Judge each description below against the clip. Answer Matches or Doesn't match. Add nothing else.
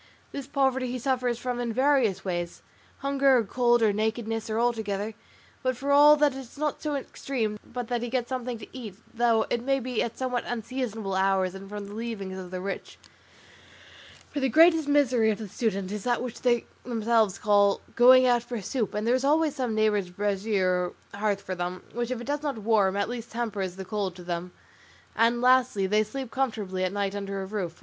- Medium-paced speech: Doesn't match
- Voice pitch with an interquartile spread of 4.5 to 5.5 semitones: Doesn't match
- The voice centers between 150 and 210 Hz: Doesn't match